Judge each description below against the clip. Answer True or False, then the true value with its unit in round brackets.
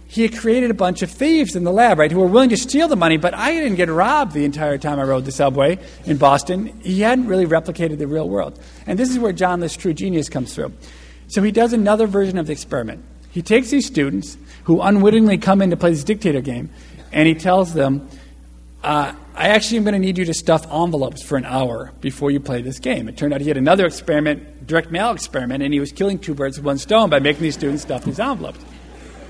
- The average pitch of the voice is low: False (165 Hz)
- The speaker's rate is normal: False (245 wpm)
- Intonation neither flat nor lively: False (6.0 semitones)